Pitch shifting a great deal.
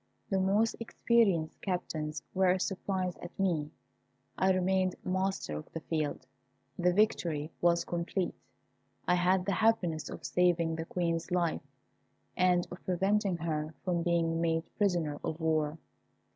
No: narrow, 2.5 semitones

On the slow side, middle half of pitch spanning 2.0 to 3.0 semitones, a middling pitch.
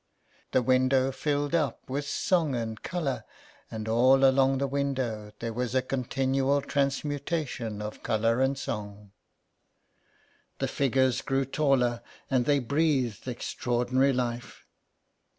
No: slow, 120 wpm; narrow, 2.6 semitones; low, 130 Hz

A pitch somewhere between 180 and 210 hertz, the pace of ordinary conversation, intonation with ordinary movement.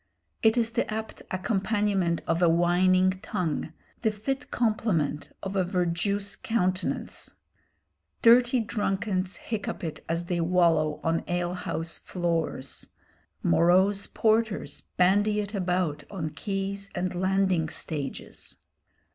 No: medium, 185 Hz; slow, 115 wpm; average, 3.3 semitones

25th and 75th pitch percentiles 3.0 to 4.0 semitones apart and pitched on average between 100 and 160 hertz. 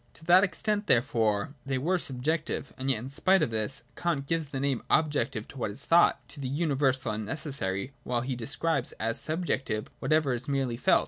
No: average, 4.8 semitones; low, 135 Hz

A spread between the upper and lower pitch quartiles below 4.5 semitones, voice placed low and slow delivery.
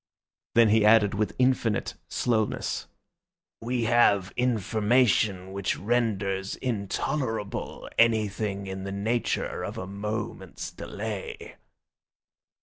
Yes: average, 2.8 semitones; low, 105 Hz; slow, 95 wpm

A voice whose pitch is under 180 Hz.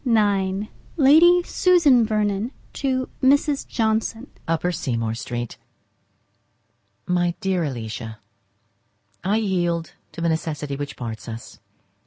No: high, 190 Hz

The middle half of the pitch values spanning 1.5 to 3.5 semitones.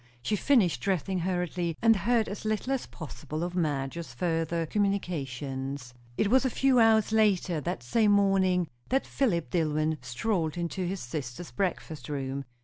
No: average, 5.2 semitones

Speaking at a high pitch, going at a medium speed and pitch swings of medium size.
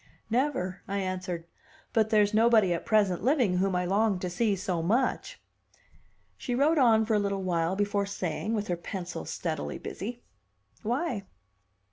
Yes: high, 200 Hz; average, 155 wpm; average, 3.8 semitones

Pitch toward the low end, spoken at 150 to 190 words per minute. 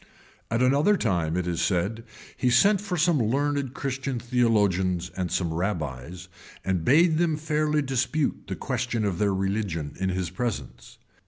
Yes: low, 110 Hz; average, 160 wpm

